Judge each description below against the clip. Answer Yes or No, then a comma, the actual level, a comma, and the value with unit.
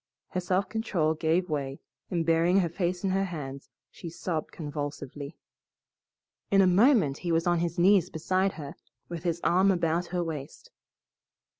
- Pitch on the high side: No, medium, 170 Hz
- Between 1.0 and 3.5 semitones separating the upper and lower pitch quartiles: Yes, average, 2.8 semitones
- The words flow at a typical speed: Yes, average, 160 wpm